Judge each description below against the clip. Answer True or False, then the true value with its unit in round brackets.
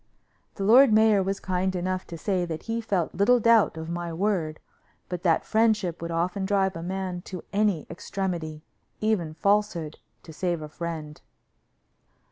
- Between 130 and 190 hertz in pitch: True (185 Hz)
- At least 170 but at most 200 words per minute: False (160 wpm)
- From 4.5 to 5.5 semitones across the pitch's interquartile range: False (3.5 semitones)